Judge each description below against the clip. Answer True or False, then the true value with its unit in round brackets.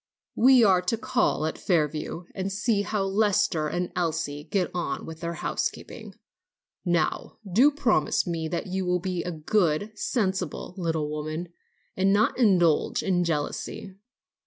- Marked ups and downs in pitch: False (3.9 semitones)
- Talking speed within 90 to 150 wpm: True (145 wpm)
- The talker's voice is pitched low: False (180 Hz)